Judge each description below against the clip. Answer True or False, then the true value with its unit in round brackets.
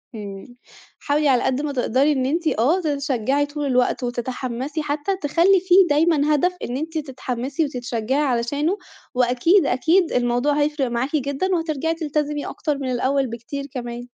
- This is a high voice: True (280 Hz)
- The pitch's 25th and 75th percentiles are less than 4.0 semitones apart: True (3.5 semitones)